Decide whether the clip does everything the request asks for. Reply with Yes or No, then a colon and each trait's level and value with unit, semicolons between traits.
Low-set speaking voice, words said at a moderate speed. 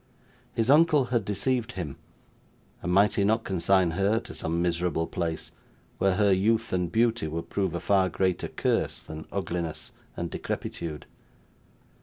Yes: very low, 95 Hz; average, 150 wpm